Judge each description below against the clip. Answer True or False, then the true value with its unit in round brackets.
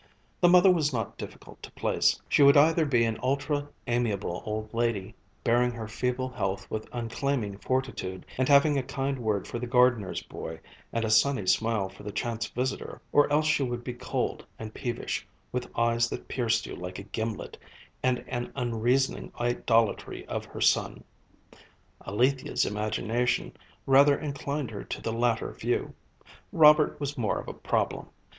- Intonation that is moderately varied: True (3.8 semitones)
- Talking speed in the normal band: True (165 wpm)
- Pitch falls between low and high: False (120 Hz)